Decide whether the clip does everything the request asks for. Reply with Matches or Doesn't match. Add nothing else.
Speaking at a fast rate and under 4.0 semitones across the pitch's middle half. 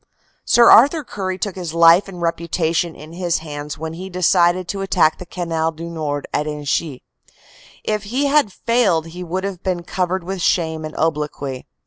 Doesn't match